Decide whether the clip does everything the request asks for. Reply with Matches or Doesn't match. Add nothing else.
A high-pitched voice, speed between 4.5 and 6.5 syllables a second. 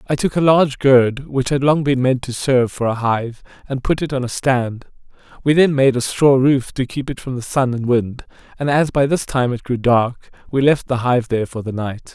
Doesn't match